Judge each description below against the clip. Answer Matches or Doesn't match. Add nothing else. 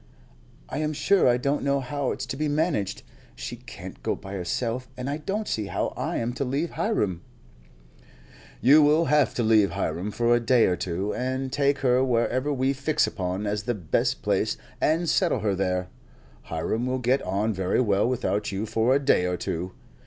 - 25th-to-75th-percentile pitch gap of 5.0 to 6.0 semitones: Matches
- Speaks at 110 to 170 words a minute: Doesn't match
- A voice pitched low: Matches